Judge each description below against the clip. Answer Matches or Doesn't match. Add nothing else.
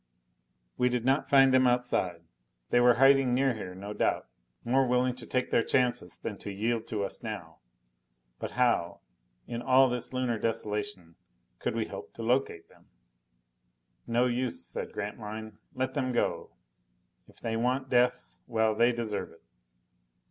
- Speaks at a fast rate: Doesn't match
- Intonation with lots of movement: Doesn't match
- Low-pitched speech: Matches